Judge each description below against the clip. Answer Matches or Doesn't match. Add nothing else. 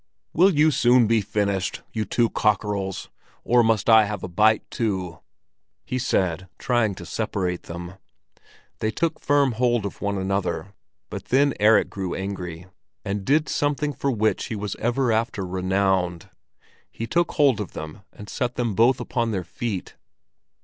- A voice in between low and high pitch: Doesn't match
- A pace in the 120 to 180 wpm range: Matches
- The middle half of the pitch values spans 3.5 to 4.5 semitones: Matches